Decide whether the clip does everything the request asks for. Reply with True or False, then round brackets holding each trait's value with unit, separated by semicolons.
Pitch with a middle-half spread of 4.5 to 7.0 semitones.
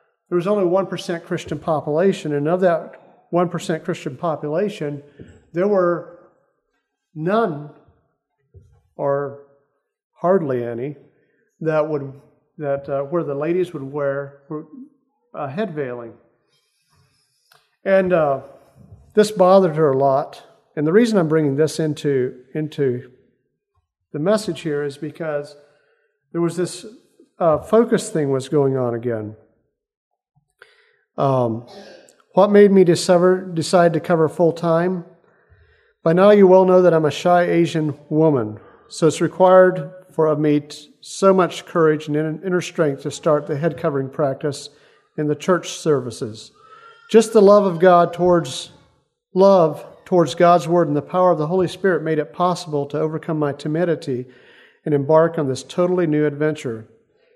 False (4.0 semitones)